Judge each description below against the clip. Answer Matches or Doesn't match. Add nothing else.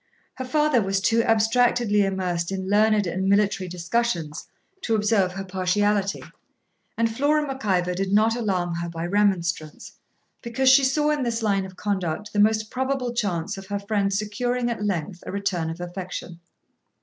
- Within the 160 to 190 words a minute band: Matches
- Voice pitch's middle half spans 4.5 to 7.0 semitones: Doesn't match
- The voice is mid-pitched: Doesn't match